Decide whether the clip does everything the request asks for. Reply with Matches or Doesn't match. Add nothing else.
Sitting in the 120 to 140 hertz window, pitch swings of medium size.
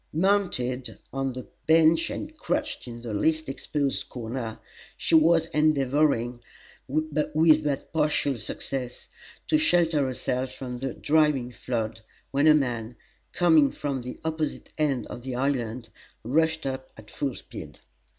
Matches